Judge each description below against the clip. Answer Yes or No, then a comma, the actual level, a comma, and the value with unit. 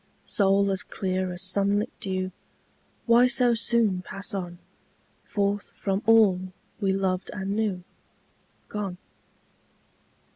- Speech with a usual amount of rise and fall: No, narrow, 1.8 semitones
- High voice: Yes, high, 195 Hz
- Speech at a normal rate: No, slow, 110 wpm